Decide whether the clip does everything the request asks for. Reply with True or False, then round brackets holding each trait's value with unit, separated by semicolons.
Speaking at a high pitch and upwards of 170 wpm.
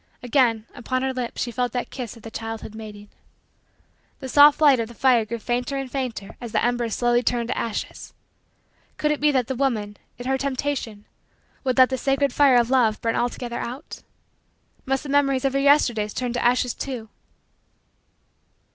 True (245 Hz; 185 wpm)